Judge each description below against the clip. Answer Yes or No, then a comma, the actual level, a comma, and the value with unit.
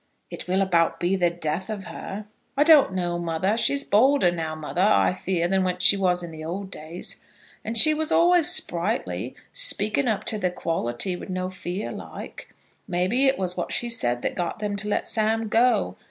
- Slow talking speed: No, average, 195 wpm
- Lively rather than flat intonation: No, average, 4.2 semitones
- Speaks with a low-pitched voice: No, high, 190 Hz